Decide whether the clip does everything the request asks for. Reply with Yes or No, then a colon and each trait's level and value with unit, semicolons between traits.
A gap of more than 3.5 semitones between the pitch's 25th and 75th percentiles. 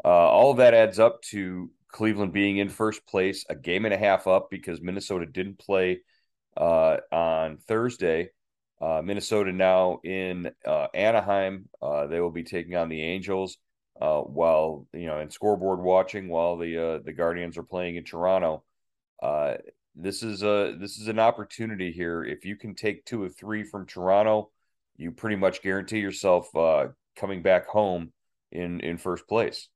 No: average, 3.2 semitones